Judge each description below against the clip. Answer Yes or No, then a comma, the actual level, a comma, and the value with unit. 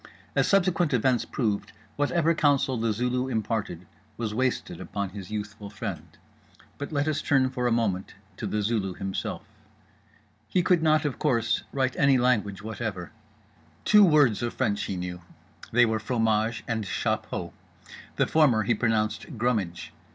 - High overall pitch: No, low, 115 Hz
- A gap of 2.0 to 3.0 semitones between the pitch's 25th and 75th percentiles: No, average, 4.2 semitones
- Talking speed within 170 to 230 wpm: No, average, 150 wpm